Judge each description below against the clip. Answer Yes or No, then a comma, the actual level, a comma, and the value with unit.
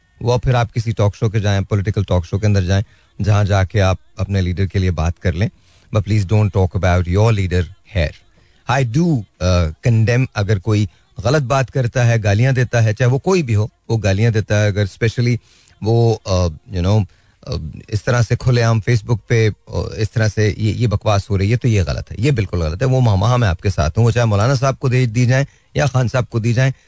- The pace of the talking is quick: Yes, fast, 230 wpm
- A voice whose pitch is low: Yes, low, 110 Hz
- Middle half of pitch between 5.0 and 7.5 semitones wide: No, average, 3.7 semitones